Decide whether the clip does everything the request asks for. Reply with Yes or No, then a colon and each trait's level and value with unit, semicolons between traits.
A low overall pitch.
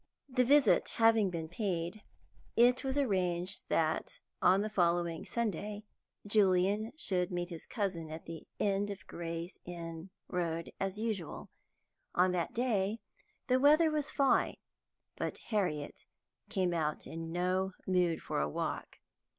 No: medium, 185 Hz